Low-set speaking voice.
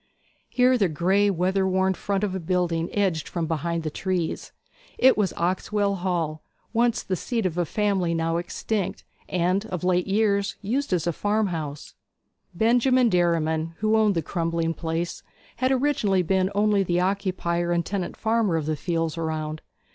No: medium, 185 Hz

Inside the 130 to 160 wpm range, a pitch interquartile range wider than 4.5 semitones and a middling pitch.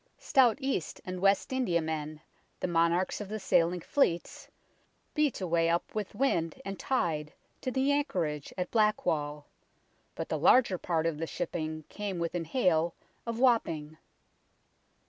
Yes: average, 145 wpm; average, 5.2 semitones; medium, 175 Hz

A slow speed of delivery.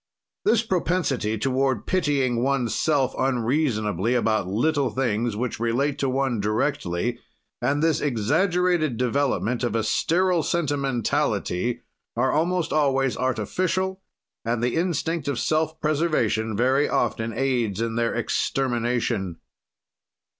Yes: slow, 110 wpm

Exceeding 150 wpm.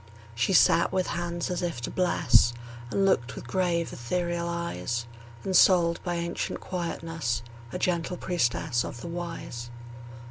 No: average, 140 wpm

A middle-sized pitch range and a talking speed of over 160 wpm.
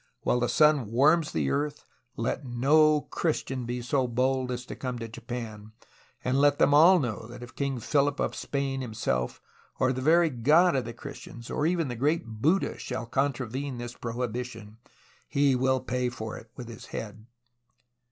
Yes: average, 3.3 semitones; average, 180 wpm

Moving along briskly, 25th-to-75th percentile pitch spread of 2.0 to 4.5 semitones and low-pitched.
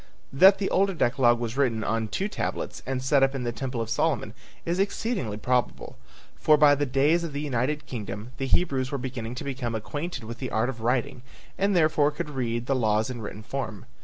Yes: fast, 210 wpm; average, 3.9 semitones; low, 130 Hz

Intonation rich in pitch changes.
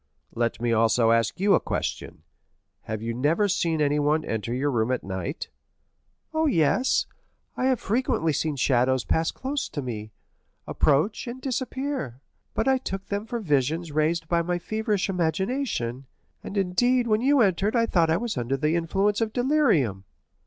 Yes: wide, 9.0 semitones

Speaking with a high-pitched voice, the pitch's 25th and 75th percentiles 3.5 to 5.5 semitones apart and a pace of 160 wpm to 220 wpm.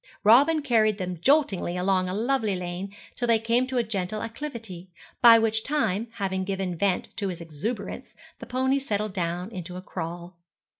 Yes: high, 205 Hz; average, 4.4 semitones; average, 170 wpm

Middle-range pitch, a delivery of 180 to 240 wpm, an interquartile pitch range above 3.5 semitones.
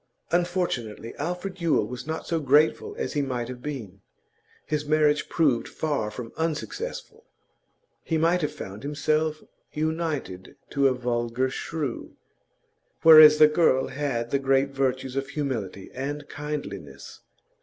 No: medium, 145 Hz; slow, 135 wpm; average, 3.9 semitones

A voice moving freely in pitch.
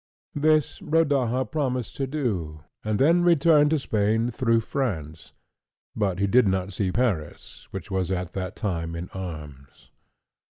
Yes: wide, 6.8 semitones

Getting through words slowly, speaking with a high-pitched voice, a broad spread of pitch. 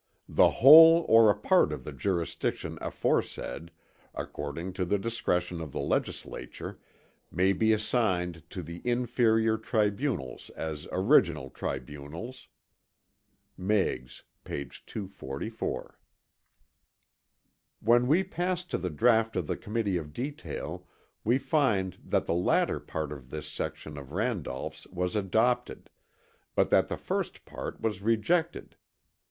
No: slow, 125 wpm; low, 100 Hz; wide, 6.0 semitones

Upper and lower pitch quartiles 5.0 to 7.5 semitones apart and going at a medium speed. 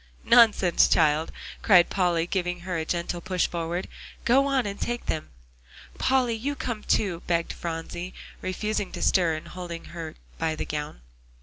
No: average, 4.1 semitones; average, 160 wpm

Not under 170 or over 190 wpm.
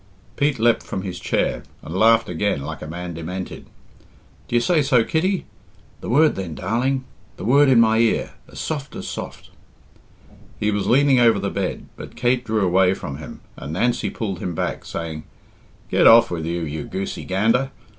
Yes: average, 185 wpm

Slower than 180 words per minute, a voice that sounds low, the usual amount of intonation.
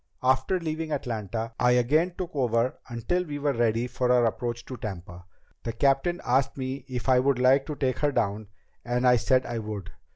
No: average, 195 wpm; low, 125 Hz; average, 3.0 semitones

